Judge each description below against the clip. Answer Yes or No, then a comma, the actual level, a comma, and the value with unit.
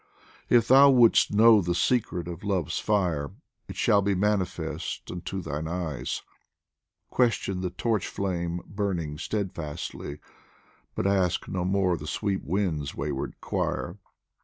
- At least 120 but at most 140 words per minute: Yes, slow, 135 wpm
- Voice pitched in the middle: No, very low, 90 Hz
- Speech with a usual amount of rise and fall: Yes, average, 3.5 semitones